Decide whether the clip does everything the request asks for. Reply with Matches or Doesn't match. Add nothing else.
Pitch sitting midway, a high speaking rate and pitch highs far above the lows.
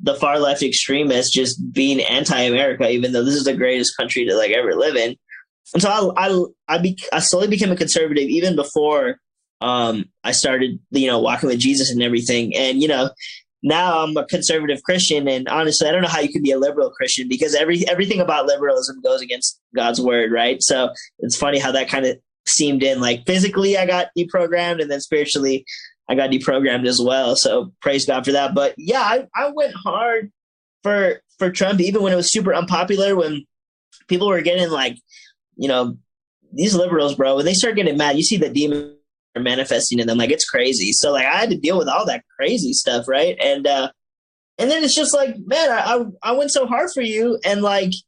Matches